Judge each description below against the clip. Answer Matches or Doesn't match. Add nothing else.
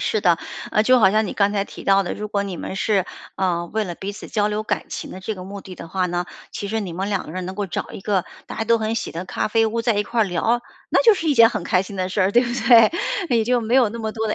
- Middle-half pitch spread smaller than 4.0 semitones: Matches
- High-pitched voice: Matches